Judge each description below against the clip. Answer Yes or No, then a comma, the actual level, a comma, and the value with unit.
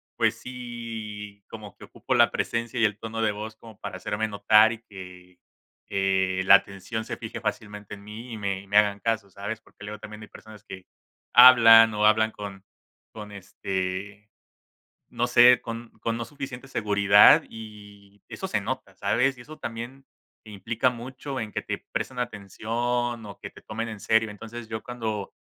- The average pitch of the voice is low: Yes, low, 110 Hz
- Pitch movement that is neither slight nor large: No, narrow, 2.3 semitones